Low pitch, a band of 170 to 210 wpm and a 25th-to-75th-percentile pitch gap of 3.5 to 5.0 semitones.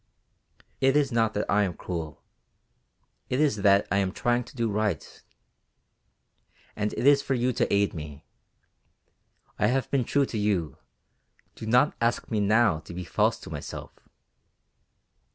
No: low, 110 Hz; average, 155 wpm; average, 4.0 semitones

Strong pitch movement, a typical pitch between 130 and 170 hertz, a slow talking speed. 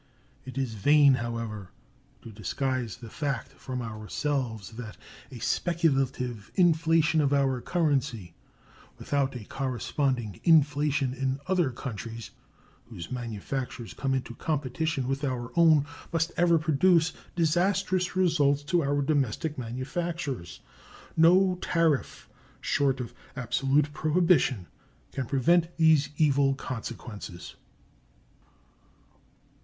No: average, 4.5 semitones; low, 135 Hz; slow, 105 wpm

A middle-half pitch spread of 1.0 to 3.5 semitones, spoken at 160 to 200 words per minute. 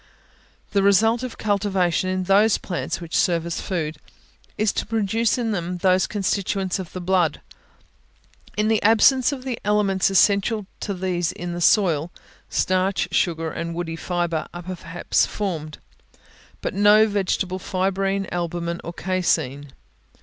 No: average, 2.9 semitones; average, 140 wpm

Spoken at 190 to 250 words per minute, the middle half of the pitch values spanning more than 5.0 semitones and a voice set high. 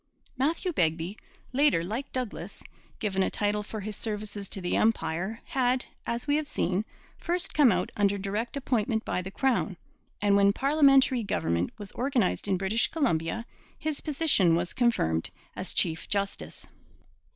No: average, 150 wpm; wide, 5.5 semitones; high, 215 Hz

